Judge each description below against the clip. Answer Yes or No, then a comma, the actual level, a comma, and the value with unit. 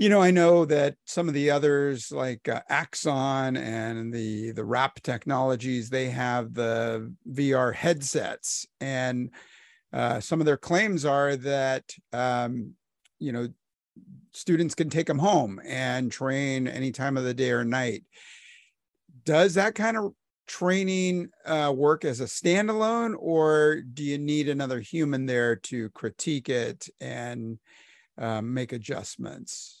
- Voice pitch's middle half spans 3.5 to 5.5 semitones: Yes, average, 4.2 semitones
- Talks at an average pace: Yes, average, 145 wpm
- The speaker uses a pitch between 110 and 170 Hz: Yes, low, 135 Hz